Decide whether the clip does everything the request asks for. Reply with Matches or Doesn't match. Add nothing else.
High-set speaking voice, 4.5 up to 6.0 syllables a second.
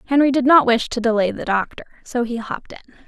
Doesn't match